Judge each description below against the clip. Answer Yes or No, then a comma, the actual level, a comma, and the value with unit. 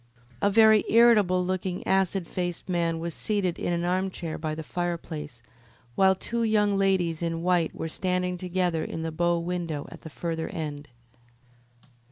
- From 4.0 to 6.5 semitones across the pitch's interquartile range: No, narrow, 2.5 semitones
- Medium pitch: Yes, medium, 175 Hz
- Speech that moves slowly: No, average, 160 wpm